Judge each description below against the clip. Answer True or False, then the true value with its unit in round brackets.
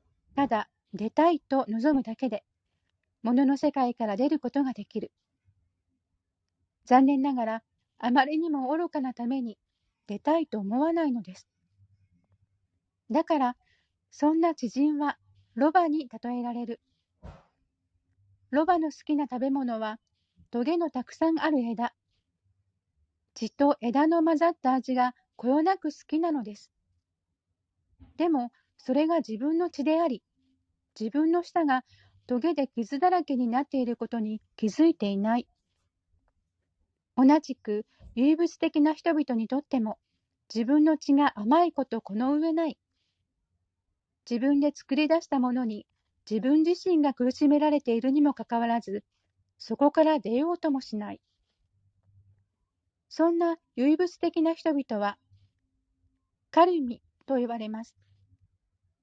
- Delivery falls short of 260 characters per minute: True (240 characters per minute)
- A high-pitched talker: True (240 Hz)